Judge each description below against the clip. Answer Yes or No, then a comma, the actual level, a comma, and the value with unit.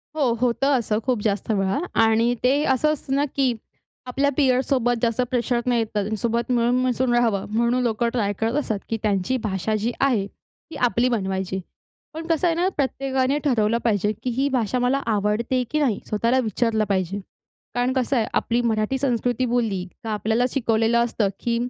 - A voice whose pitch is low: No, high, 235 Hz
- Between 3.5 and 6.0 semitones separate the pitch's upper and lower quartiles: No, average, 2.9 semitones